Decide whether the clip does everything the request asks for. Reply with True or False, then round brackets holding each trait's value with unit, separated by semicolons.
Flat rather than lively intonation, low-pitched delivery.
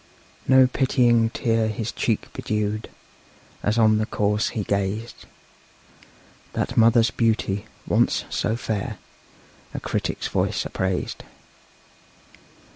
True (1.9 semitones; 110 Hz)